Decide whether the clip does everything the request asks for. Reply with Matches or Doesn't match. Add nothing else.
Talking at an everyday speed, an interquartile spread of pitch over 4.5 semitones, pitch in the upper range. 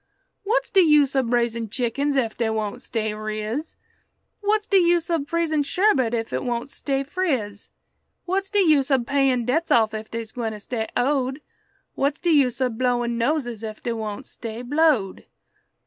Matches